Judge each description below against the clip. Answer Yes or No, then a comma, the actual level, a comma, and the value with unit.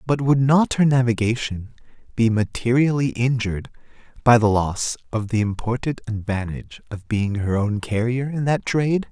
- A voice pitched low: Yes, low, 120 Hz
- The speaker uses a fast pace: No, average, 150 wpm